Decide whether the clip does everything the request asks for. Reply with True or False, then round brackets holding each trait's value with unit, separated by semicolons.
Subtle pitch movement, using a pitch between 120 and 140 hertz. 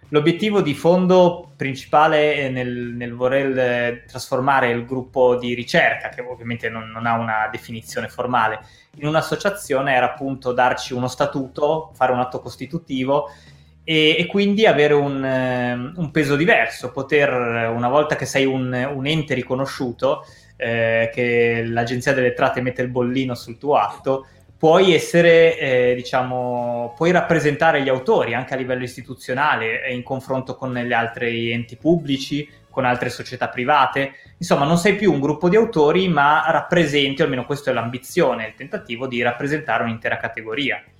False (3.5 semitones; 130 Hz)